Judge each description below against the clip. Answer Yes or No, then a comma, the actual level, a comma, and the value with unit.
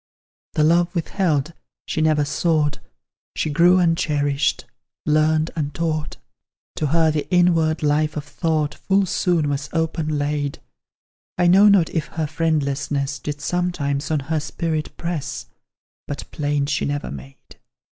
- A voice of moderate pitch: Yes, medium, 155 Hz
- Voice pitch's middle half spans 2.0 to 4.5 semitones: Yes, narrow, 2.4 semitones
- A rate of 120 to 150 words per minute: Yes, slow, 135 wpm